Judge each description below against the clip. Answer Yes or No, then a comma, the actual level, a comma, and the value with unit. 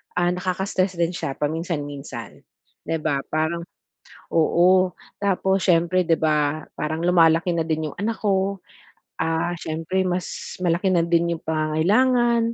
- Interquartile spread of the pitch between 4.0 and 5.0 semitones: No, average, 2.7 semitones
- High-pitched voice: No, medium, 170 Hz